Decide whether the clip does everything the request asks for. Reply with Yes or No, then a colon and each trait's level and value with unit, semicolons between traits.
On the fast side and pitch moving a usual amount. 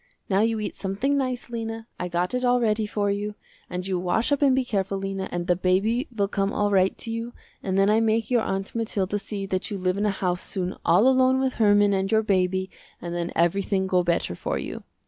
Yes: fast, 235 wpm; average, 3.3 semitones